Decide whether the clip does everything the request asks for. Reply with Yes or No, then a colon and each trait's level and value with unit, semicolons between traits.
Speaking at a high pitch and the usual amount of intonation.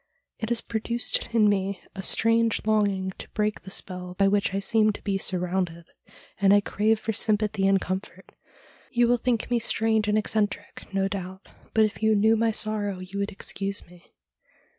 No: high, 205 Hz; narrow, 2.3 semitones